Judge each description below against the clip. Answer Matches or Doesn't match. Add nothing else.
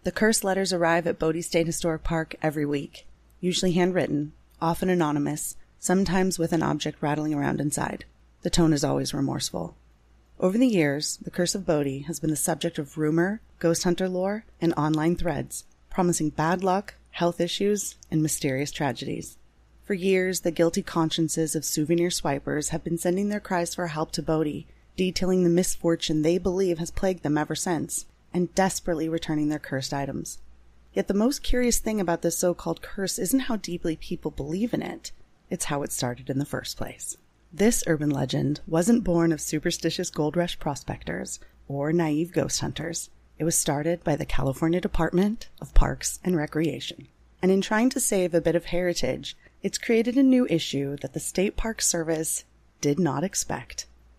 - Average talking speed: Matches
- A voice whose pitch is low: Doesn't match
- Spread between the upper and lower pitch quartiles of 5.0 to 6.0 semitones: Doesn't match